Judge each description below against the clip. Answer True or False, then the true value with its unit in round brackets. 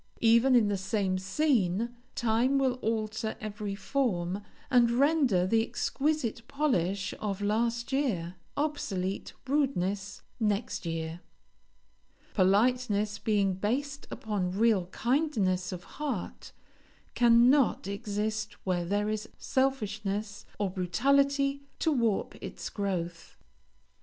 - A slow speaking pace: True (105 wpm)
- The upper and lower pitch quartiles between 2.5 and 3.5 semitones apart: False (4.7 semitones)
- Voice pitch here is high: True (215 Hz)